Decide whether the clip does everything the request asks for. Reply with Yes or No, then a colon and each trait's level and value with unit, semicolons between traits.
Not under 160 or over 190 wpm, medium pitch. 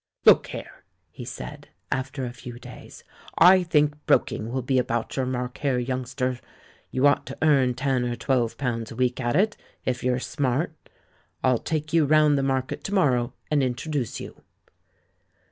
No: average, 170 wpm; low, 130 Hz